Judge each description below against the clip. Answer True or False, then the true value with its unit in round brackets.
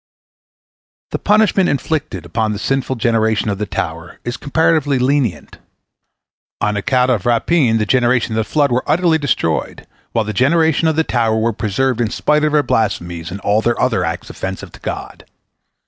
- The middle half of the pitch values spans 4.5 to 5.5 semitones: True (5.2 semitones)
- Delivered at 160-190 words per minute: True (175 wpm)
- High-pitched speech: False (120 Hz)